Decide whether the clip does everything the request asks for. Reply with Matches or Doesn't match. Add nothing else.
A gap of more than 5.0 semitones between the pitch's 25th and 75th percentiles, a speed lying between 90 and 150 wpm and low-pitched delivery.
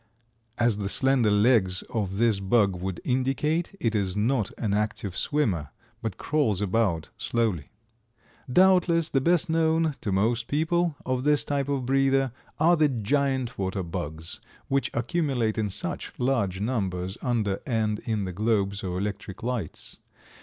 Matches